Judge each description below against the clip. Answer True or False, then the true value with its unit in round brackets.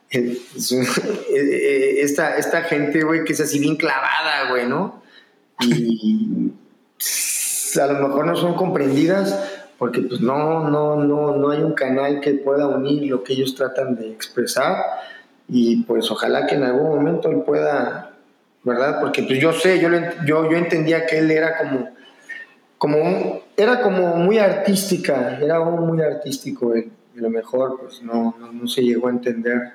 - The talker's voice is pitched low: False (145 Hz)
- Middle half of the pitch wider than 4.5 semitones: True (4.9 semitones)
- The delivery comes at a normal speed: True (160 wpm)